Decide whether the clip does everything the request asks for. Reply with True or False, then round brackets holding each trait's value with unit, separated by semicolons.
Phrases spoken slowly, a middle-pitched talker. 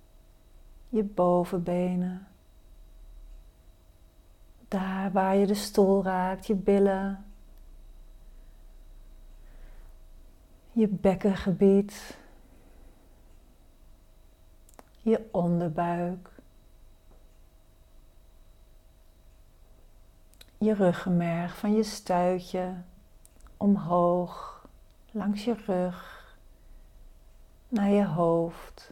True (55 wpm; 165 Hz)